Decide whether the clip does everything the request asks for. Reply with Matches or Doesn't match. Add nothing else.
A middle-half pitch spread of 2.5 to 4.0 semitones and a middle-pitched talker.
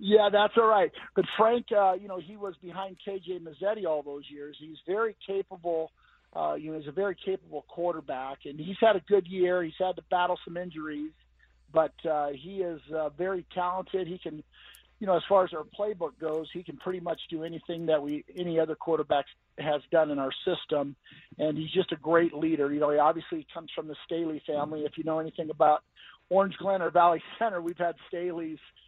Matches